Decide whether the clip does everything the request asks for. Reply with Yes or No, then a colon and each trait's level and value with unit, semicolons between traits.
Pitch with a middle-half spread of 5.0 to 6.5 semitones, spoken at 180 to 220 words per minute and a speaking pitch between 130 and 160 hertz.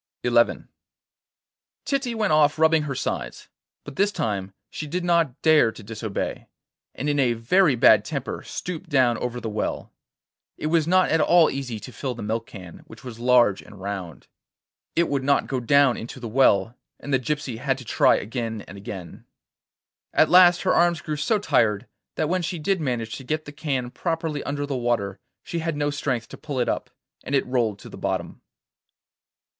Yes: wide, 5.5 semitones; average, 190 wpm; low, 135 Hz